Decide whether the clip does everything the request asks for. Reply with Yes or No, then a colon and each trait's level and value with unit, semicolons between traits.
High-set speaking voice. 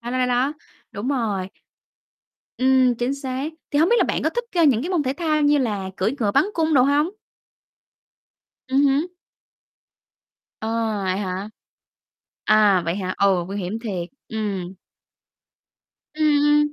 Yes: high, 245 Hz